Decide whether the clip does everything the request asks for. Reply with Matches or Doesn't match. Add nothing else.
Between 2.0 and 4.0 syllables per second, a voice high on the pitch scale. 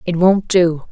Doesn't match